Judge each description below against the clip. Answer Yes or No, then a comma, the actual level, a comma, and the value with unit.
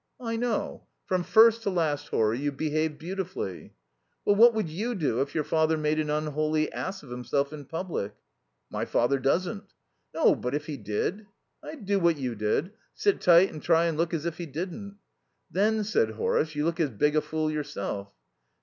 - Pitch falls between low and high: Yes, medium, 155 Hz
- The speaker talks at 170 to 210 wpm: Yes, average, 190 wpm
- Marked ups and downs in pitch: No, average, 4.6 semitones